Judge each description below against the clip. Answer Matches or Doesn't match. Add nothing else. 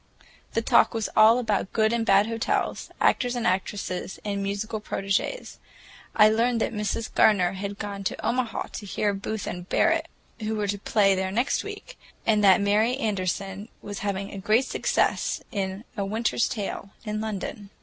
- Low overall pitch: Doesn't match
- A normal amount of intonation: Doesn't match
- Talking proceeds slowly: Doesn't match